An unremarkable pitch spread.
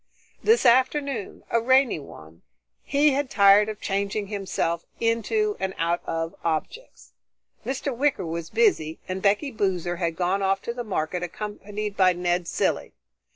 No: wide, 6.2 semitones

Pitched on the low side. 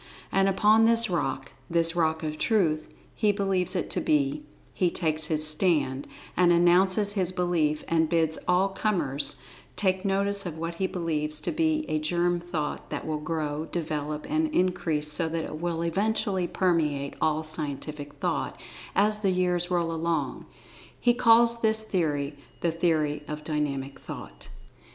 No: medium, 170 Hz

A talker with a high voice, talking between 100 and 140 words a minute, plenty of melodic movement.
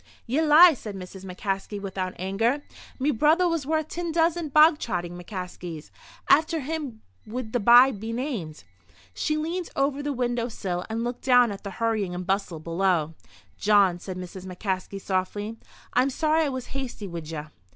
No: high, 225 Hz; average, 170 wpm; wide, 7.4 semitones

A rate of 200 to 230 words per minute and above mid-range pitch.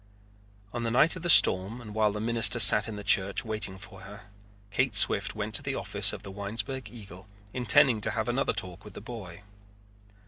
No: fast, 205 wpm; low, 105 Hz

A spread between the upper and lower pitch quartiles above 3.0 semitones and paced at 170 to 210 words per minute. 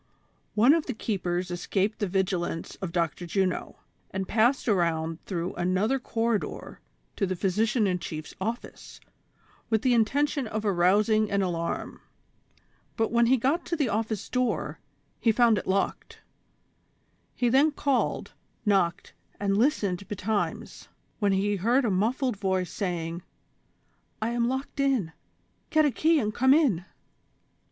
No: average, 4.7 semitones; average, 145 wpm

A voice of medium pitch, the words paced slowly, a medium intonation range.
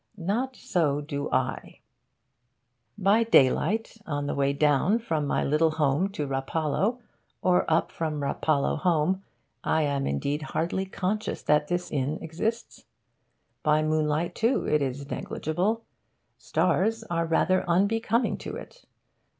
Yes: medium, 160 Hz; slow, 130 wpm; average, 4.9 semitones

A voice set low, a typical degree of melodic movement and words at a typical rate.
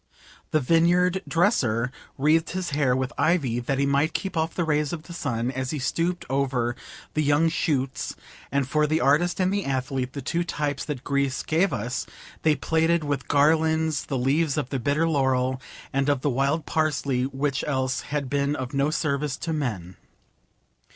No: medium, 145 Hz; average, 3.4 semitones; average, 180 wpm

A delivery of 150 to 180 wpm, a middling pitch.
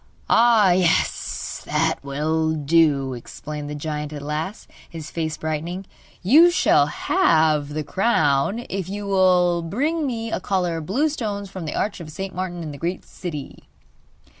Yes: average, 160 wpm; medium, 170 Hz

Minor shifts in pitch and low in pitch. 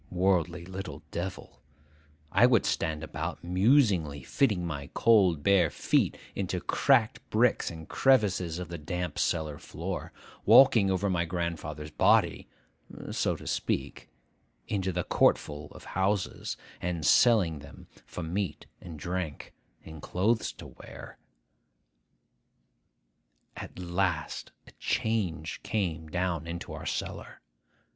No: average, 3.5 semitones; very low, 90 Hz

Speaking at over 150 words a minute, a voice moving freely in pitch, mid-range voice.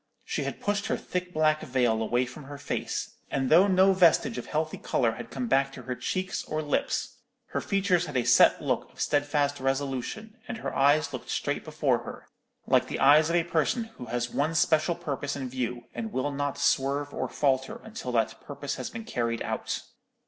No: average, 200 wpm; average, 4.8 semitones; medium, 145 Hz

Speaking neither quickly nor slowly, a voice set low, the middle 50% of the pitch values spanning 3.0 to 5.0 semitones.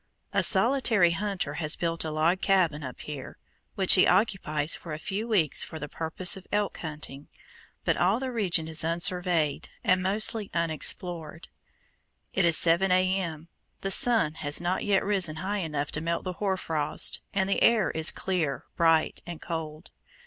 No: average, 170 wpm; medium, 175 Hz; average, 3.5 semitones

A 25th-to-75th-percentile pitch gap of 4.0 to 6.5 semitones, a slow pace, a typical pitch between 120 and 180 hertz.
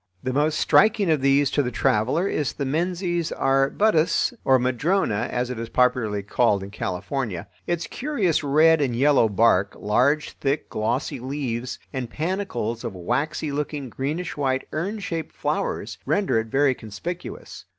No: average, 5.2 semitones; average, 150 wpm; low, 135 Hz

